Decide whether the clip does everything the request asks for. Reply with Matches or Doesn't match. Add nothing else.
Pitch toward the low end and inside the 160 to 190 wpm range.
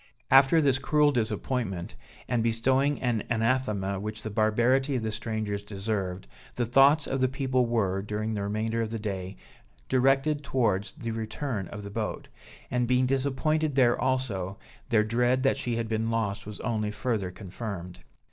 Matches